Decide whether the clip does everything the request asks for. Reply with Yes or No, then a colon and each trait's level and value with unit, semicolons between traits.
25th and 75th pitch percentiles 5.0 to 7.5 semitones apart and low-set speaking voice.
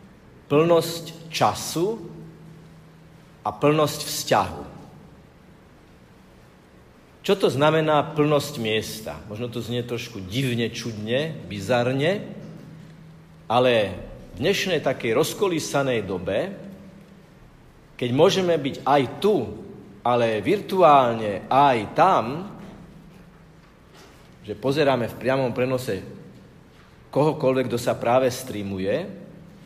No: average, 5.3 semitones; medium, 150 Hz